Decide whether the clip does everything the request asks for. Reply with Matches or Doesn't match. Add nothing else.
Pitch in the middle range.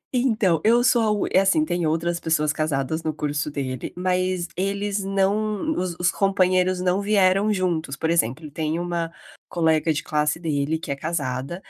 Matches